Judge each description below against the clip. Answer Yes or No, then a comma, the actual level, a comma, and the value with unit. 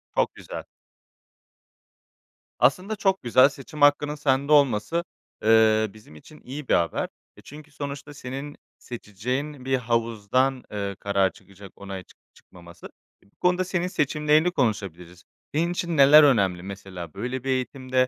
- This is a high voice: No, low, 130 Hz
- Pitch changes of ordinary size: No, wide, 6.3 semitones